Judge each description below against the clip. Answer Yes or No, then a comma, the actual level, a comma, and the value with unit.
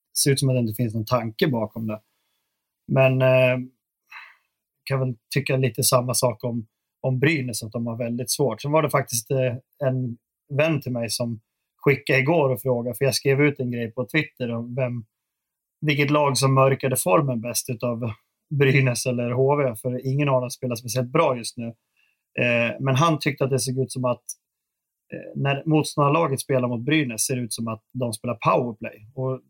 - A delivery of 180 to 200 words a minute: Yes, fast, 195 wpm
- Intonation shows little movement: Yes, narrow, 2.2 semitones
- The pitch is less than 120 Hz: No, low, 130 Hz